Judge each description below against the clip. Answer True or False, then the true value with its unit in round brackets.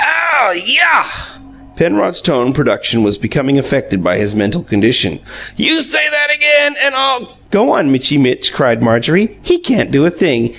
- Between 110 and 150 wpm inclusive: False (170 wpm)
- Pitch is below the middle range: False (150 Hz)